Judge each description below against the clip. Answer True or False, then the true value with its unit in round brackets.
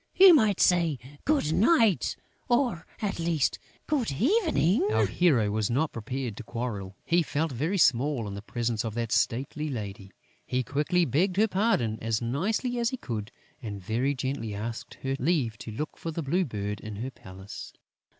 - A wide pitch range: True (7.9 semitones)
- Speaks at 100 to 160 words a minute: False (175 wpm)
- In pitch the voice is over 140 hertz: False (135 Hz)